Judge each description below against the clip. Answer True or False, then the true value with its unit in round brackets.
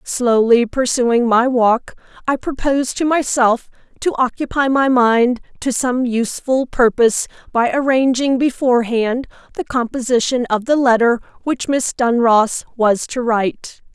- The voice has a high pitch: True (245 Hz)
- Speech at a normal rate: False (130 wpm)